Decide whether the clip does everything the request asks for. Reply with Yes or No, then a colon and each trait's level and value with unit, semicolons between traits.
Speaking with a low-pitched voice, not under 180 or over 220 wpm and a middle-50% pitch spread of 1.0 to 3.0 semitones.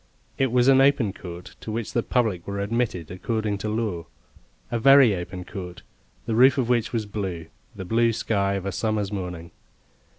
No: low, 105 Hz; average, 185 wpm; average, 4.0 semitones